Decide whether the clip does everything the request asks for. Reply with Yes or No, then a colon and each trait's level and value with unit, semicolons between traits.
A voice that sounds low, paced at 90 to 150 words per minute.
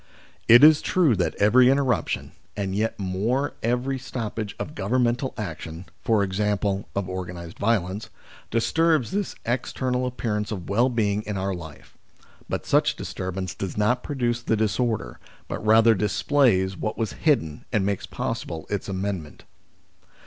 Yes: low, 105 Hz; average, 140 wpm